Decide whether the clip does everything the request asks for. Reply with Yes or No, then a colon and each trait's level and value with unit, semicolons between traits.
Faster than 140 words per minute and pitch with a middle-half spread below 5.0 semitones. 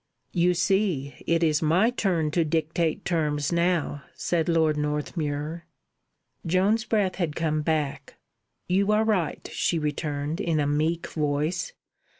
No: slow, 135 wpm; average, 3.1 semitones